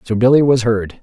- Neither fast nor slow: No, fast, 235 wpm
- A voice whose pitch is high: No, low, 120 Hz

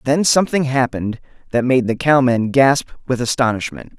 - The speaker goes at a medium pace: Yes, average, 150 wpm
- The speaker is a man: Yes, male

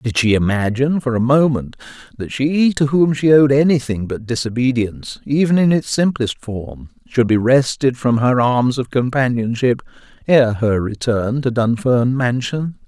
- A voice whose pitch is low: Yes, low, 125 Hz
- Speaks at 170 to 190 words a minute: No, average, 160 wpm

